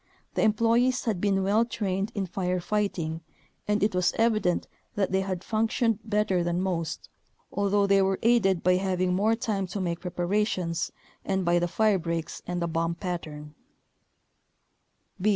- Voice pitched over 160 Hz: Yes, high, 190 Hz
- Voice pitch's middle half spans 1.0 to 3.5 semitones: Yes, average, 3.1 semitones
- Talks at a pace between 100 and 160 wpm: Yes, average, 155 wpm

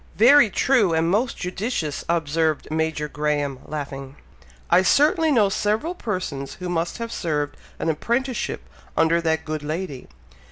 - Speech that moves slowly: No, average, 145 wpm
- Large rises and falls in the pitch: Yes, wide, 6.4 semitones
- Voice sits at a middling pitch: Yes, medium, 165 Hz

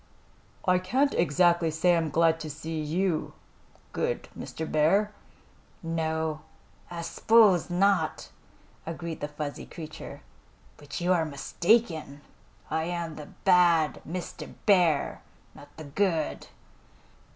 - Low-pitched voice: No, medium, 165 Hz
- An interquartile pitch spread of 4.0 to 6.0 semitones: No, narrow, 2.6 semitones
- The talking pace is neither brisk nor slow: No, slow, 115 wpm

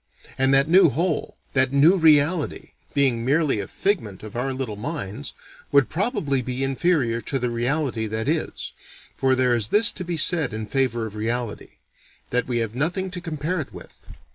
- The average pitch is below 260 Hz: Yes, low, 135 Hz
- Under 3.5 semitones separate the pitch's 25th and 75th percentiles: No, average, 5.2 semitones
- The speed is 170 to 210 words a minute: Yes, average, 180 wpm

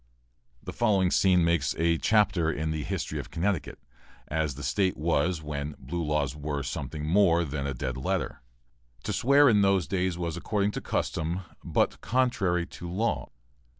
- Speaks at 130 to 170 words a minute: Yes, average, 165 wpm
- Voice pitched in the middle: No, very low, 85 Hz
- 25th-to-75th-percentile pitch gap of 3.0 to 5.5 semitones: Yes, average, 4.2 semitones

